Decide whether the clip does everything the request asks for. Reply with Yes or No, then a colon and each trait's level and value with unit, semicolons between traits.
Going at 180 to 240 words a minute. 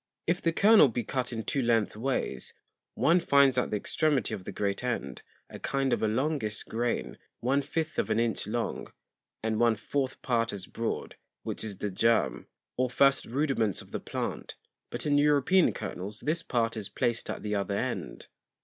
Yes: average, 185 wpm